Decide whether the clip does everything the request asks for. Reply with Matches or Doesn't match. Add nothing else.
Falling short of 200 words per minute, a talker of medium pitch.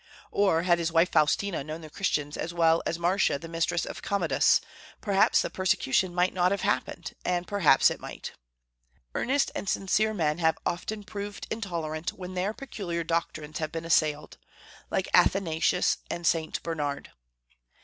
Matches